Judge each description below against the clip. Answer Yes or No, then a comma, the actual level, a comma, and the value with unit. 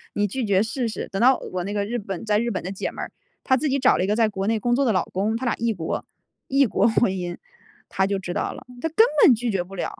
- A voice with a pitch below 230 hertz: Yes, high, 215 Hz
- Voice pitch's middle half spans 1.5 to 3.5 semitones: No, average, 3.9 semitones